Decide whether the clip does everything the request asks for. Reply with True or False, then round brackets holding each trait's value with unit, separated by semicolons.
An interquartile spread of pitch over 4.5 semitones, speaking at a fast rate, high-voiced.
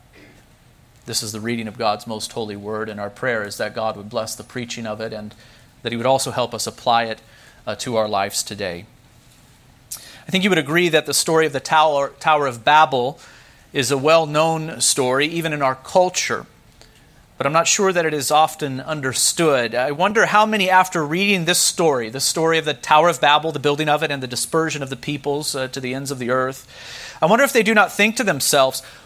False (4.9 semitones; 220 wpm; 140 Hz)